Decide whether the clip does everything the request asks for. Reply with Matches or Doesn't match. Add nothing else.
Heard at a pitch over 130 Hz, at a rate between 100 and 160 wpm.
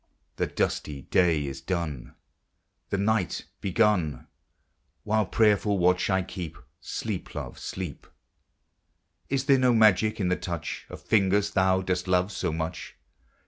Doesn't match